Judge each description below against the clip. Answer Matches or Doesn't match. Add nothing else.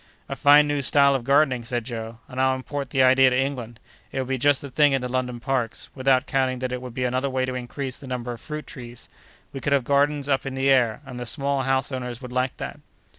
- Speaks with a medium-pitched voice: Doesn't match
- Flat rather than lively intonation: Matches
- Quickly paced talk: Matches